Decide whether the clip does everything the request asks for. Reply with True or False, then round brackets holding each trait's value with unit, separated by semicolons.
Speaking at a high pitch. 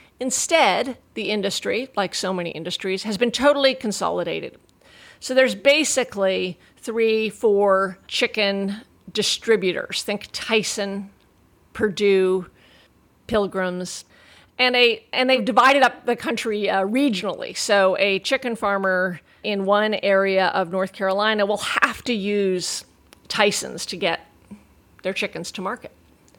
True (205 Hz)